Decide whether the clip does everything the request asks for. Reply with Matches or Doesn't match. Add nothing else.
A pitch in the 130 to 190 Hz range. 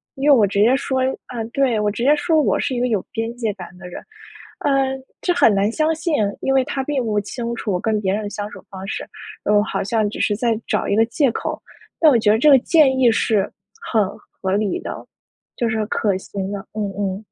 Doesn't match